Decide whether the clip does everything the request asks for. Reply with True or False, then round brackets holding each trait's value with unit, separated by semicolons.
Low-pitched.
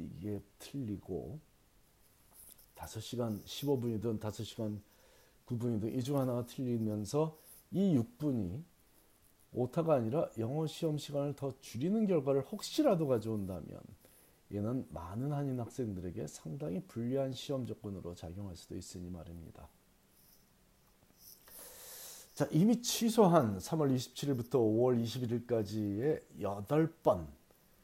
True (120 Hz)